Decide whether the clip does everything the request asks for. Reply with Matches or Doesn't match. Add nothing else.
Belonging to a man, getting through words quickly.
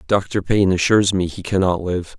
Doesn't match